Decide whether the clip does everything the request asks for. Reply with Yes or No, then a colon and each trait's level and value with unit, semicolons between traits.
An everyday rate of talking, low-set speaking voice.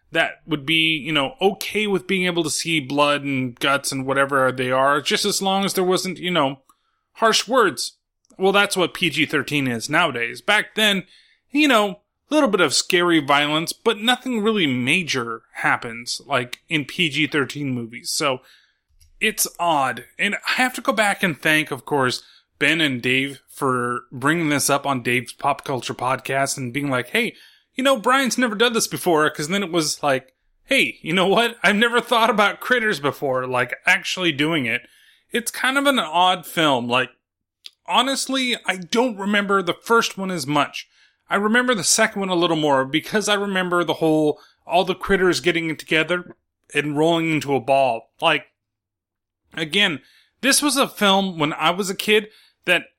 No: average, 180 wpm; medium, 165 Hz